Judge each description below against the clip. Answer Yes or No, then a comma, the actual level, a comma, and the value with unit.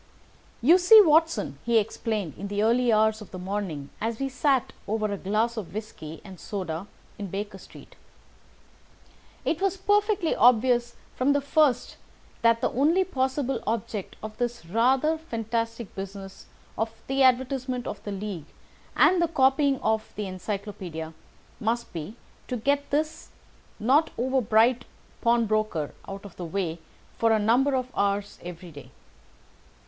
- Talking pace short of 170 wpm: Yes, average, 150 wpm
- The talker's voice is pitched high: Yes, high, 230 Hz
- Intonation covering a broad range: No, average, 4.8 semitones